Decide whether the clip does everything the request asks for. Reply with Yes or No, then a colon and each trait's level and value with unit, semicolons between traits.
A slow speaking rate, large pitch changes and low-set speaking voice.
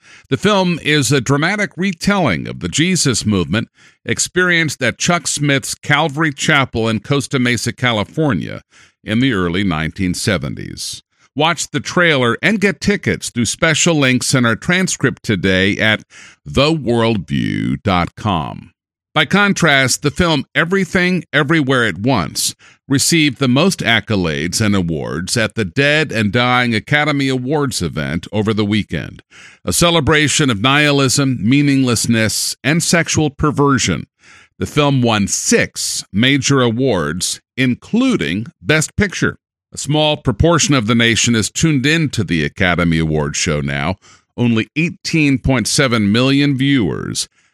Yes: slow, 125 wpm; wide, 6.0 semitones; low, 130 Hz